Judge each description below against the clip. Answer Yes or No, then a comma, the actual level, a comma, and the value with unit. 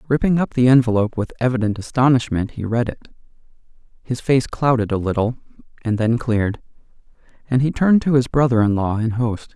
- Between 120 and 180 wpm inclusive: Yes, average, 175 wpm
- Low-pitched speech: Yes, low, 120 Hz